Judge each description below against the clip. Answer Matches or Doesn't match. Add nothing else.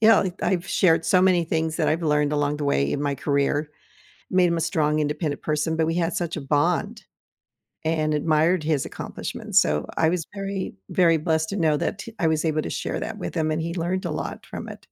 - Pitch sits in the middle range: Matches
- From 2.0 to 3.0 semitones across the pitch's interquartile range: Matches